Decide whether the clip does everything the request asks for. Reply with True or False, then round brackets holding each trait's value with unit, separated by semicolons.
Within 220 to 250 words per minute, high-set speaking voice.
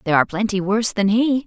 True (245 wpm; 210 Hz)